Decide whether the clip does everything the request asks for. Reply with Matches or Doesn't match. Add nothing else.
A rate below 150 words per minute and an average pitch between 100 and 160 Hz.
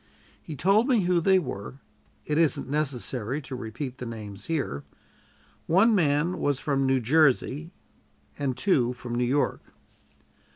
Matches